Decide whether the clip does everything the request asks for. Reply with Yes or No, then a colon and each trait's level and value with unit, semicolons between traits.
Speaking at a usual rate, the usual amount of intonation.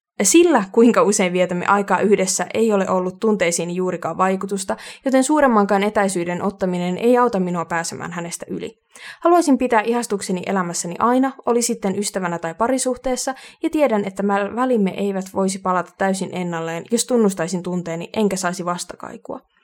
Yes: average, 145 wpm; average, 4.5 semitones